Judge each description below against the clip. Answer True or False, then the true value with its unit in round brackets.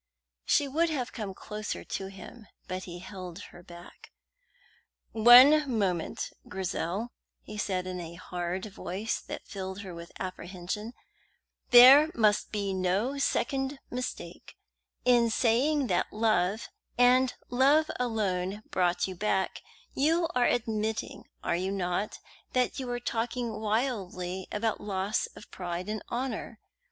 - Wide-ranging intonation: False (4.8 semitones)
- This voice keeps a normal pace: False (130 wpm)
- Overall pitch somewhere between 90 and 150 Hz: False (210 Hz)